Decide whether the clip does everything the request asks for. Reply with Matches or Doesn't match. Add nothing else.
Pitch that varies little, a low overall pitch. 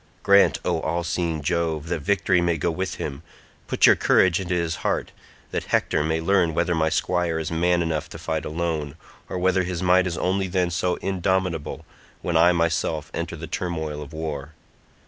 Matches